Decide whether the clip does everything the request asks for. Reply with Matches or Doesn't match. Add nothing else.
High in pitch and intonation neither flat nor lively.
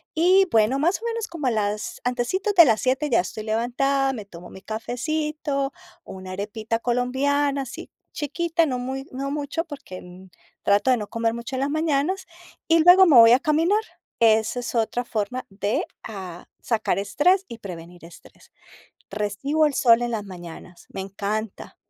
Doesn't match